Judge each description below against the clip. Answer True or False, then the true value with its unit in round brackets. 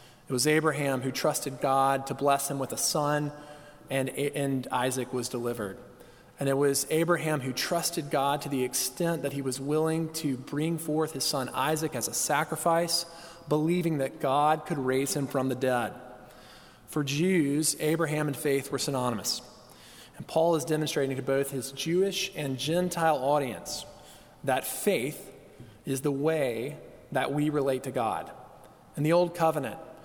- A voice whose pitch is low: False (145 Hz)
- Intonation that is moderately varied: True (3.0 semitones)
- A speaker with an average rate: True (160 wpm)